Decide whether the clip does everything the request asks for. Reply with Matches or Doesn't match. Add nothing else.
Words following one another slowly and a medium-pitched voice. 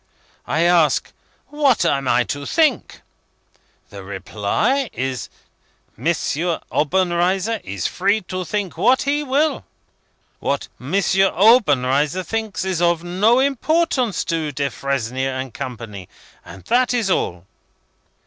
Matches